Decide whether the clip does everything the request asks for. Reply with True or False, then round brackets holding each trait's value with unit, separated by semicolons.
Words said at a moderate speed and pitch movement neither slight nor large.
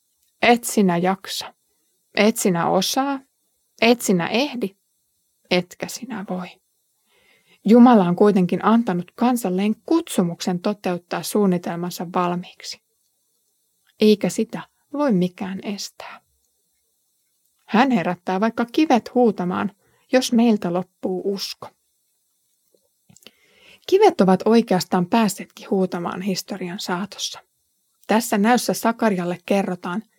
False (90 wpm; 4.0 semitones)